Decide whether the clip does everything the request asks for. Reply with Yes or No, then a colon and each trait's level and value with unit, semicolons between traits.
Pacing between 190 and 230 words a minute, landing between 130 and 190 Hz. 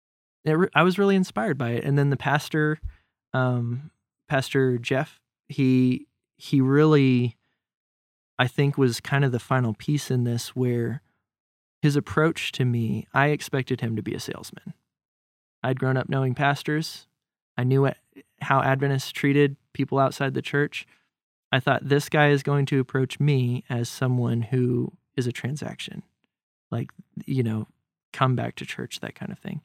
No: average, 160 wpm; low, 135 Hz